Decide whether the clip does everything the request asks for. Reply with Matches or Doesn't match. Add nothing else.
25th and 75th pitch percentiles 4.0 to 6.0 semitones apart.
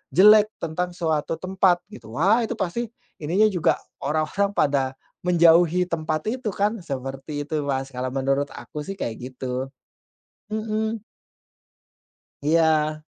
Matches